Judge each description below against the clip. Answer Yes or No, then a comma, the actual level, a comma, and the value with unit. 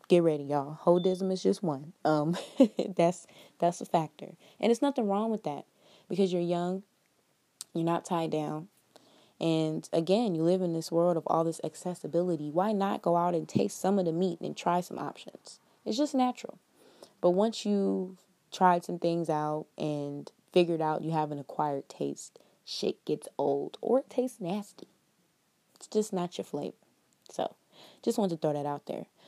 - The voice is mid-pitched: Yes, medium, 175 Hz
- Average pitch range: Yes, average, 3.5 semitones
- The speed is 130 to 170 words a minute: No, average, 180 wpm